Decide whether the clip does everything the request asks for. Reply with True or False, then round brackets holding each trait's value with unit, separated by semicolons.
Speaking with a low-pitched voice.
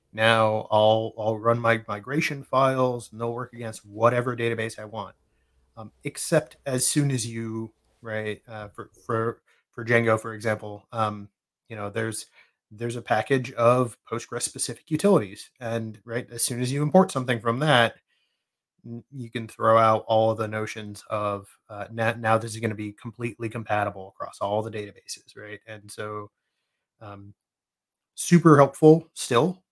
True (115 Hz)